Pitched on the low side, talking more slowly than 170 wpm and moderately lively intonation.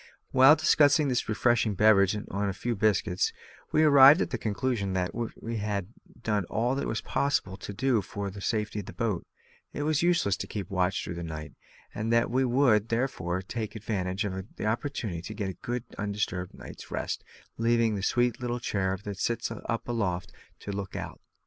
No: low, 110 Hz; average, 195 wpm; average, 3.7 semitones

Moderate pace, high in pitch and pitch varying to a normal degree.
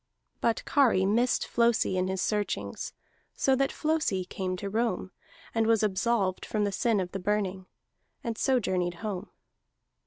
Yes: average, 155 wpm; high, 210 Hz; average, 3.7 semitones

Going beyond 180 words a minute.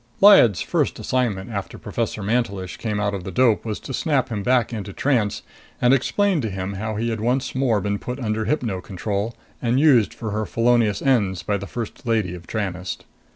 Yes: average, 200 wpm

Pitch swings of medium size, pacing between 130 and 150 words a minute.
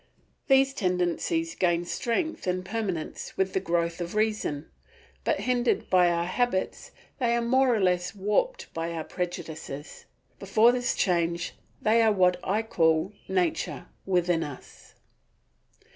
Yes: average, 5.0 semitones; slow, 135 wpm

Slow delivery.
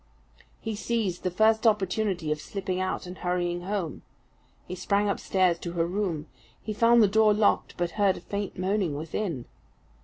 No: average, 165 wpm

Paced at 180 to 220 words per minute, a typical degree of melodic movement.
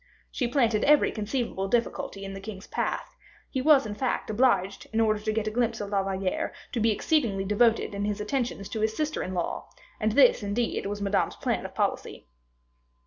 Yes: average, 195 wpm; average, 3.2 semitones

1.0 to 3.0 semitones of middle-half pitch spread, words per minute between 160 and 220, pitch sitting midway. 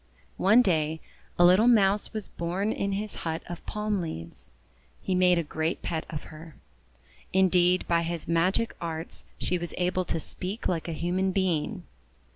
Yes: average, 2.7 semitones; average, 170 wpm; medium, 180 Hz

